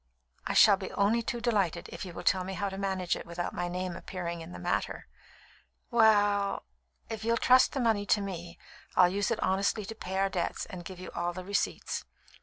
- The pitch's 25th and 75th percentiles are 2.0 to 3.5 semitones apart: Yes, average, 2.7 semitones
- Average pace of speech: No, fast, 215 wpm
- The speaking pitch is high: Yes, high, 195 Hz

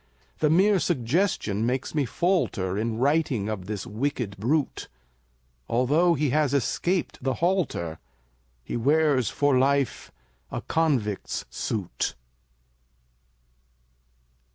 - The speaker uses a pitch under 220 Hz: Yes, low, 135 Hz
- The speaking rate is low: Yes, slow, 105 wpm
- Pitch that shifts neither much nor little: No, wide, 5.9 semitones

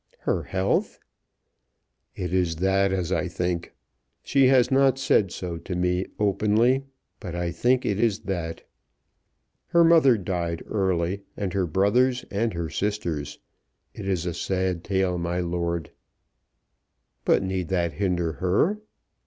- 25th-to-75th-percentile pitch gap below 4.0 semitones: Yes, average, 3.5 semitones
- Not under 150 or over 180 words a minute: No, slow, 135 wpm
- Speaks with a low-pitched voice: Yes, very low, 95 Hz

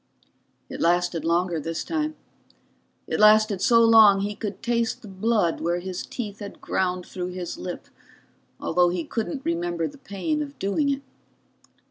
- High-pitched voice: Yes, high, 195 Hz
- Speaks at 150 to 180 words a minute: Yes, average, 155 wpm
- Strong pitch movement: No, average, 4.5 semitones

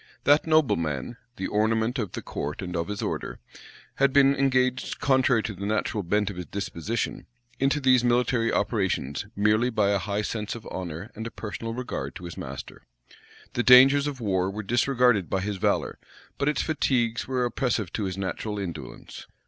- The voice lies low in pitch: Yes, low, 110 Hz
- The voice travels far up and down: No, average, 4.4 semitones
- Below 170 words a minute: No, average, 180 wpm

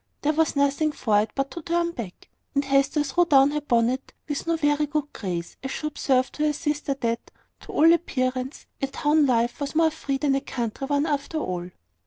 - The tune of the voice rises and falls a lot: No, average, 2.9 semitones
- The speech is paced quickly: Yes, fast, 210 wpm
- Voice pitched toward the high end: Yes, very high, 280 Hz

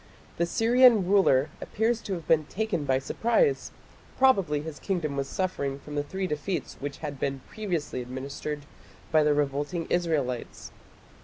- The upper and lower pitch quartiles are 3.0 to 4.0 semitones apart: No, average, 5.3 semitones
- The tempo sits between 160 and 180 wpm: No, average, 150 wpm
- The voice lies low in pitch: No, medium, 155 Hz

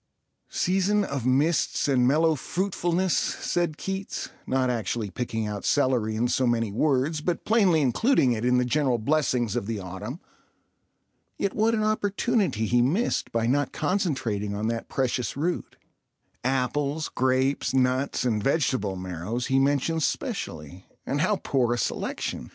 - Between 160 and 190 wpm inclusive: No, average, 145 wpm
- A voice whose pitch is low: Yes, low, 130 Hz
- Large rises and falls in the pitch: Yes, wide, 5.9 semitones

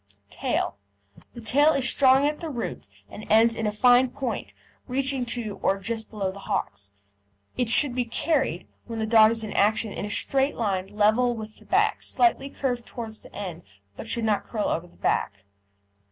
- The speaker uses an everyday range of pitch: Yes, average, 3.5 semitones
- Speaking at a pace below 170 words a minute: No, average, 190 wpm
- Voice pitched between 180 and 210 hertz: No, high, 225 Hz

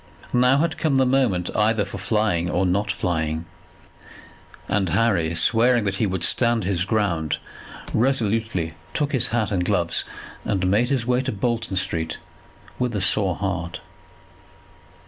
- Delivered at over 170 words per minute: No, average, 145 wpm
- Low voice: Yes, low, 105 Hz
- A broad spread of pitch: No, average, 4.6 semitones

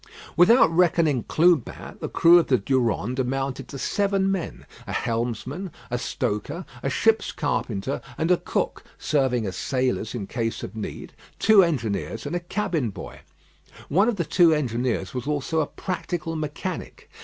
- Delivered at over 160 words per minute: No, average, 155 wpm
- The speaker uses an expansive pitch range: Yes, wide, 6.1 semitones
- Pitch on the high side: No, medium, 145 Hz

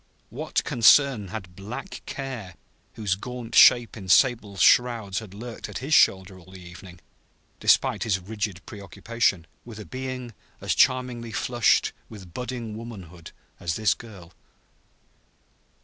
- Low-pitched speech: Yes, low, 110 Hz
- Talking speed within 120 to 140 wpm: Yes, slow, 135 wpm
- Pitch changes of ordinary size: Yes, average, 4.3 semitones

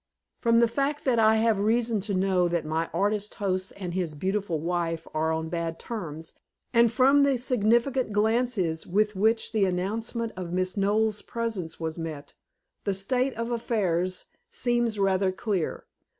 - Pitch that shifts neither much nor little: Yes, average, 4.6 semitones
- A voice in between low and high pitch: No, high, 205 Hz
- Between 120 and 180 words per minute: Yes, average, 160 wpm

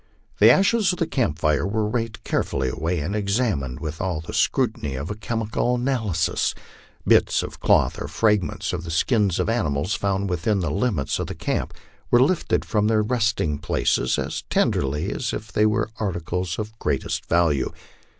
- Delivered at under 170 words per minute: No, average, 180 wpm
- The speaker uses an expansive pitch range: Yes, wide, 5.8 semitones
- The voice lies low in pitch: Yes, low, 100 Hz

